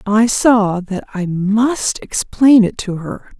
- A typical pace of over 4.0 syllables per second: No, 3.2 syllables/s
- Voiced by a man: No, female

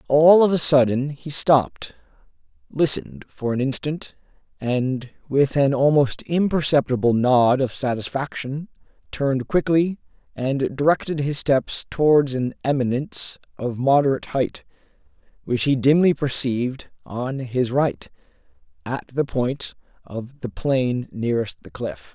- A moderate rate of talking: No, slow, 125 wpm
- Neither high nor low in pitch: No, low, 130 Hz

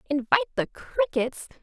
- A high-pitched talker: Yes, very high, 315 Hz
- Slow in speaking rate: Yes, slow, 110 wpm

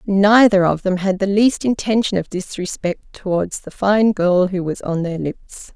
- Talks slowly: No, average, 190 wpm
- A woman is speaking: Yes, female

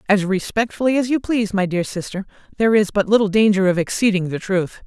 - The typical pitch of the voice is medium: No, high, 205 Hz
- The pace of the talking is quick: Yes, fast, 210 wpm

